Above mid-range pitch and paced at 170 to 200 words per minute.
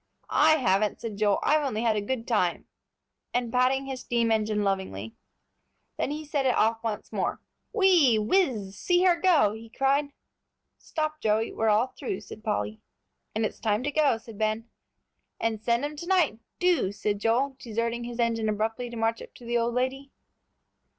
Yes: high, 230 Hz; average, 180 wpm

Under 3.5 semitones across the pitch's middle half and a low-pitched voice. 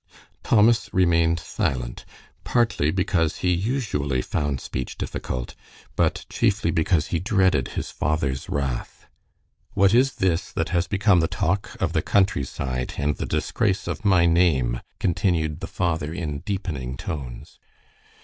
No: average, 5.2 semitones; very low, 85 Hz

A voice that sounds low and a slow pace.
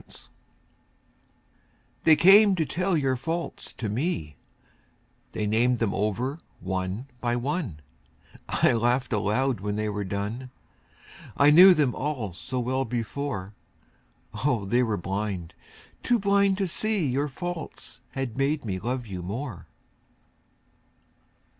Yes: low, 125 Hz; slow, 130 wpm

